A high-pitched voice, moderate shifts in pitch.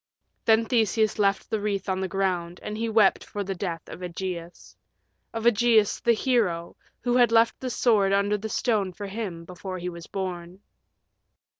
Yes: high, 200 Hz; average, 3.5 semitones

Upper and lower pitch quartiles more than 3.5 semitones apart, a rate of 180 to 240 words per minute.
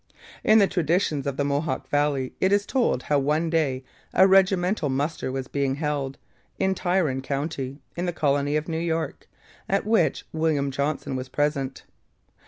No: average, 4.1 semitones; average, 165 wpm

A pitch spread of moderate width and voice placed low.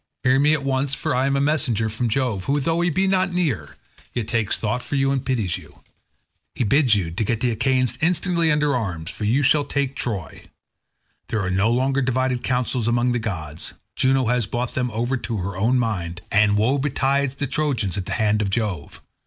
Yes: average, 4.2 semitones; low, 125 Hz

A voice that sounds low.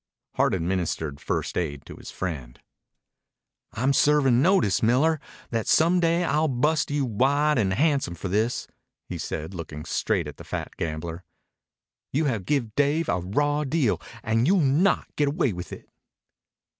Yes: low, 125 Hz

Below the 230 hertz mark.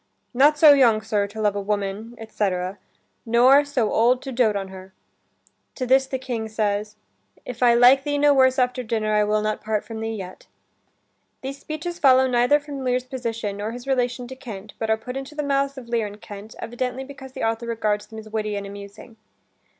No: high, 235 Hz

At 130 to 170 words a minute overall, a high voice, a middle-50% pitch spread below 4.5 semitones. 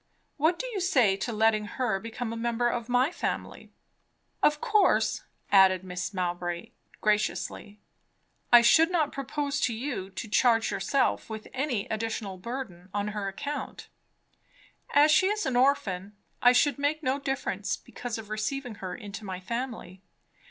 No: average, 150 wpm; high, 230 Hz; average, 5.3 semitones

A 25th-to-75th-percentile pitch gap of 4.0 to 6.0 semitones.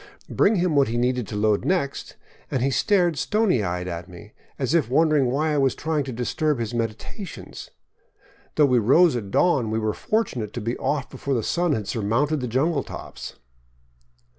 Yes: wide, 5.6 semitones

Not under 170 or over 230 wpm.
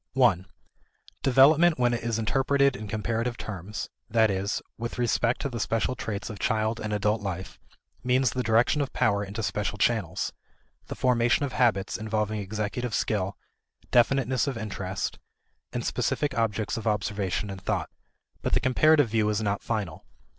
No: average, 160 wpm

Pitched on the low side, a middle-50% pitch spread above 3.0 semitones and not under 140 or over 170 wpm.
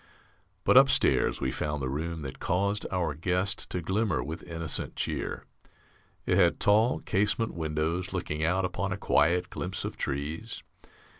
Yes: very low, 85 Hz; average, 3.6 semitones; average, 150 wpm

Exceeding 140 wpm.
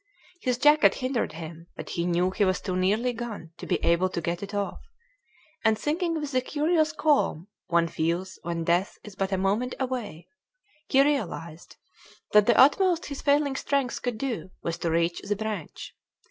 Yes: average, 180 wpm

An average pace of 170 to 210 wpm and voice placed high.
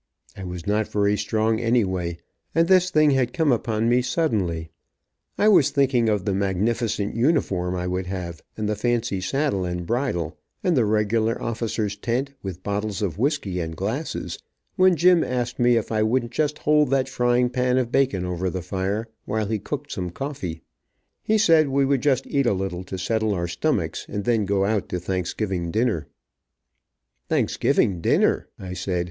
No: average, 175 wpm; low, 110 Hz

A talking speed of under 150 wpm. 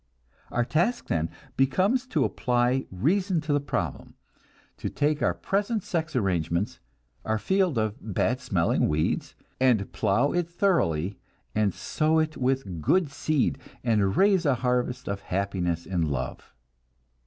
Yes: average, 140 wpm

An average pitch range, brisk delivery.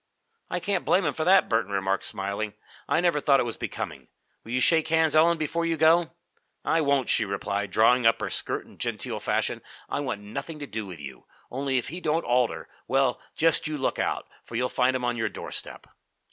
No: wide, 6.0 semitones; fast, 210 wpm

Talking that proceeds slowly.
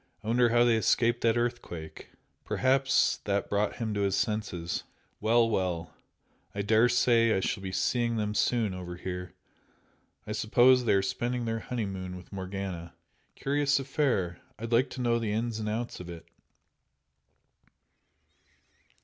No: average, 150 wpm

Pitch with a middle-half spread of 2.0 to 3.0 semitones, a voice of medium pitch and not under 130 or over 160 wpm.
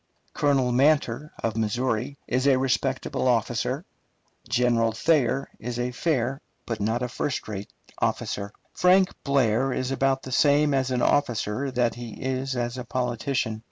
No: narrow, 2.4 semitones; low, 125 Hz; average, 145 wpm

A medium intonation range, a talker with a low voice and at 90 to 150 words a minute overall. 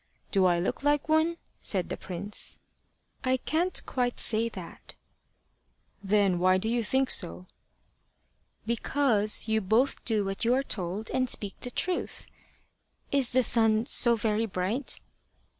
No: average, 4.8 semitones; high, 225 Hz; average, 140 wpm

